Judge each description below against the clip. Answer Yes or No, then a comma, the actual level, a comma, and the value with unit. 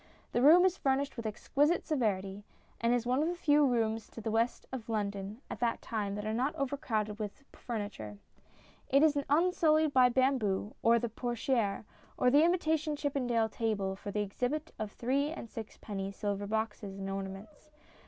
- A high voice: Yes, high, 235 Hz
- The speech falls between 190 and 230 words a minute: No, average, 175 wpm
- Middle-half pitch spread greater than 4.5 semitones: Yes, average, 5.2 semitones